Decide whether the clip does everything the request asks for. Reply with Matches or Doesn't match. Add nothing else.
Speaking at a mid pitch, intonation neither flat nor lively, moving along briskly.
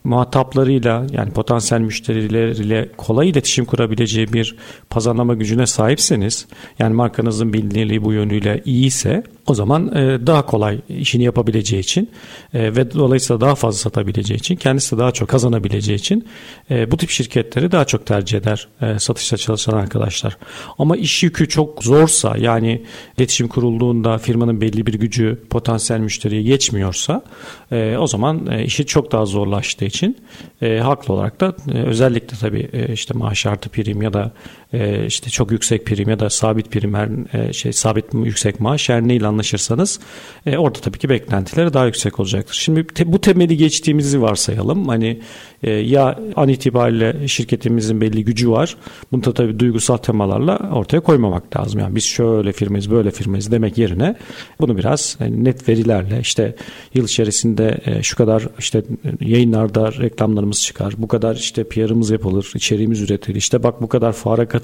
Doesn't match